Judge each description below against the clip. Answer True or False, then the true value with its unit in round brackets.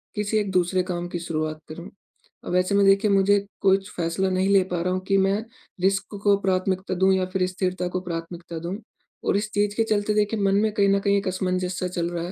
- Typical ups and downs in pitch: False (1.7 semitones)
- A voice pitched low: False (190 Hz)